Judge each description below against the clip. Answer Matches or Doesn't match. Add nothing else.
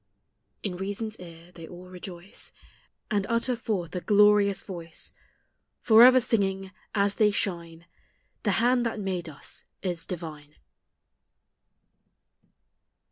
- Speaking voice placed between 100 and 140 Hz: Doesn't match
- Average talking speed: Doesn't match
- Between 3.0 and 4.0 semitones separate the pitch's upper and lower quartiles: Matches